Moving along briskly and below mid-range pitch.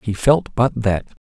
No: average, 195 wpm; low, 120 Hz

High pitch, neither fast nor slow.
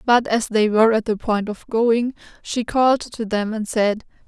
No: high, 225 Hz; fast, 210 wpm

